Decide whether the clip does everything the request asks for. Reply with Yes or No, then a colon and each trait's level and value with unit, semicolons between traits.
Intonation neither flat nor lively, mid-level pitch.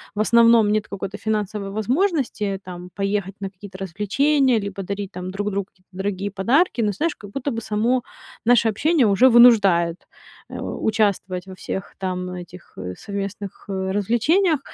No: average, 3.5 semitones; high, 205 Hz